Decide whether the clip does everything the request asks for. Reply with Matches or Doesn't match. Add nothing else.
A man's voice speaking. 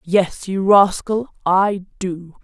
Doesn't match